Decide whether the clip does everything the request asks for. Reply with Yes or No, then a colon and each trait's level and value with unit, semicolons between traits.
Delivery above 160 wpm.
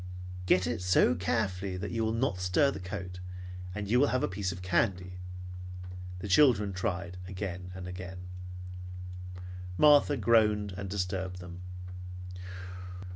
No: slow, 135 wpm